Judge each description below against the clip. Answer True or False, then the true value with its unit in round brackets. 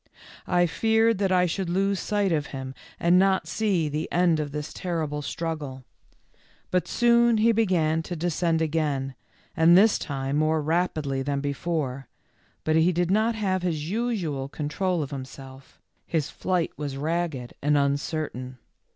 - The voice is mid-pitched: True (160 Hz)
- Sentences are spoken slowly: False (155 wpm)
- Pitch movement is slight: False (4.2 semitones)